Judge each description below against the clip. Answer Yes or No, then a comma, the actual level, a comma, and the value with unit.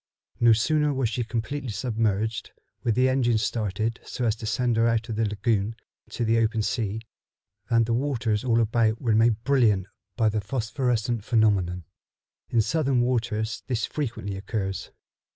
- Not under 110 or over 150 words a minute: No, average, 165 wpm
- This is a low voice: Yes, low, 115 Hz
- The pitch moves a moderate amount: No, narrow, 2.2 semitones